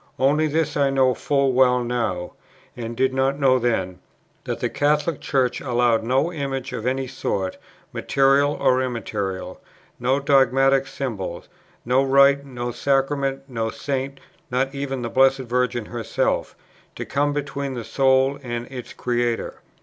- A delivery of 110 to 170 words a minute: Yes, average, 145 wpm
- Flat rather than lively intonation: Yes, narrow, 2.2 semitones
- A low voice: Yes, low, 130 Hz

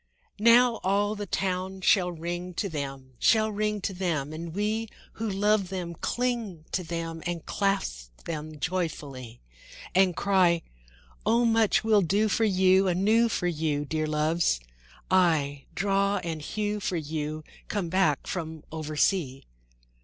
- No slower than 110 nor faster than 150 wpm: Yes, average, 140 wpm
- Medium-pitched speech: Yes, medium, 180 Hz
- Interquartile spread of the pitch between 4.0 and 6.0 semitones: Yes, average, 4.6 semitones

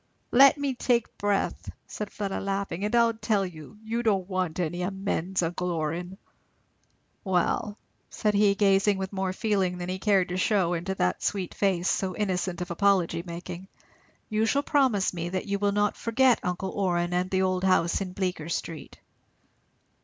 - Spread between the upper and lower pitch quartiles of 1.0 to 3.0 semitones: Yes, narrow, 2.5 semitones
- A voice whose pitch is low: No, high, 190 Hz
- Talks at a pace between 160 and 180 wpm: Yes, average, 170 wpm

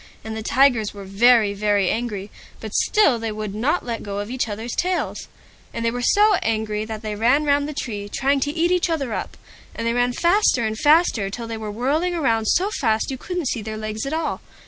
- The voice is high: Yes, high, 235 Hz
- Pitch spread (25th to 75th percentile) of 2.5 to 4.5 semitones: No, average, 5.1 semitones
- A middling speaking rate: No, fast, 230 wpm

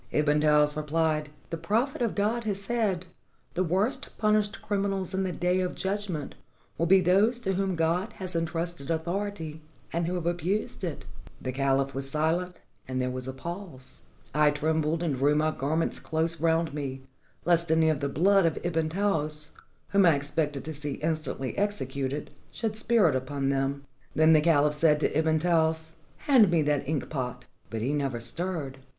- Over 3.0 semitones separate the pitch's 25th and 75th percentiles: Yes, average, 4.0 semitones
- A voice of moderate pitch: Yes, medium, 160 Hz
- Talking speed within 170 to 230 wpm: Yes, average, 185 wpm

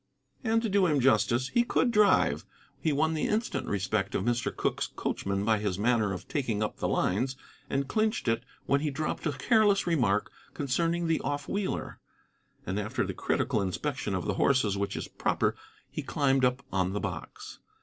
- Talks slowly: No, average, 185 wpm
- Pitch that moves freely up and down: Yes, wide, 7.9 semitones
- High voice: No, low, 135 Hz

